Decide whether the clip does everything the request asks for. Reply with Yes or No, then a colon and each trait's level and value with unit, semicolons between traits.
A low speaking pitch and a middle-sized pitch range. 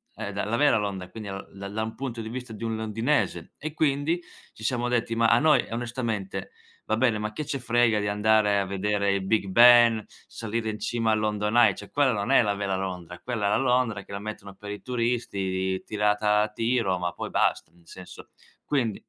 Yes: low, 110 Hz; average, 3.0 semitones